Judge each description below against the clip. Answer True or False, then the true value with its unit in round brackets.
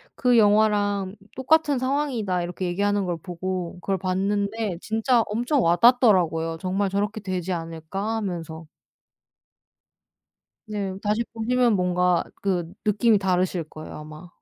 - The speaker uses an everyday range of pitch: True (3.6 semitones)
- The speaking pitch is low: False (195 Hz)